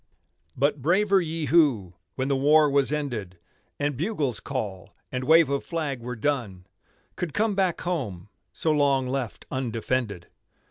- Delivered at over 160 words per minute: No, average, 145 wpm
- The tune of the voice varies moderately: Yes, average, 4.8 semitones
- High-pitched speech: No, medium, 140 Hz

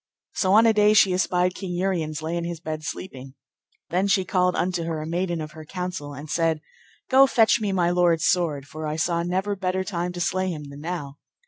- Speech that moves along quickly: Yes, fast, 220 wpm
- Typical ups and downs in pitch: Yes, average, 3.0 semitones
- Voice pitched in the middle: Yes, medium, 175 Hz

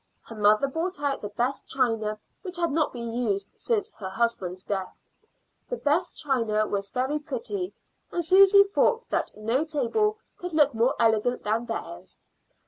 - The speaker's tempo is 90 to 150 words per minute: No, average, 160 wpm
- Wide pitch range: Yes, wide, 8.1 semitones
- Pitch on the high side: Yes, very high, 255 Hz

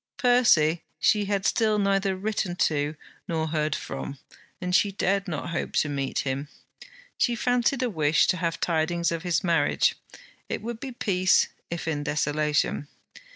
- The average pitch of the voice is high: No, medium, 175 Hz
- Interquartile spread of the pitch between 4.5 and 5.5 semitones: Yes, average, 4.8 semitones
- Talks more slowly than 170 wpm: Yes, average, 155 wpm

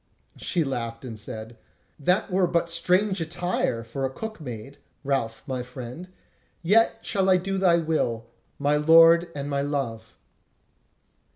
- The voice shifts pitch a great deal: Yes, wide, 6.2 semitones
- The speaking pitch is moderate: Yes, medium, 150 Hz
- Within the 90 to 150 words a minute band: Yes, average, 145 wpm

